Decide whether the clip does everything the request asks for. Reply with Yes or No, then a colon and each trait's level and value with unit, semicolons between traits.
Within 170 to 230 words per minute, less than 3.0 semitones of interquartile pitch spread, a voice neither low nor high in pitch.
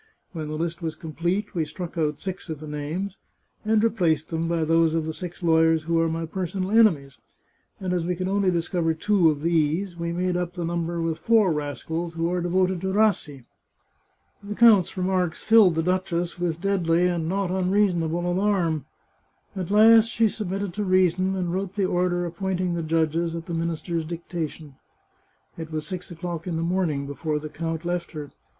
Yes: average, 185 wpm; narrow, 2.5 semitones; medium, 170 Hz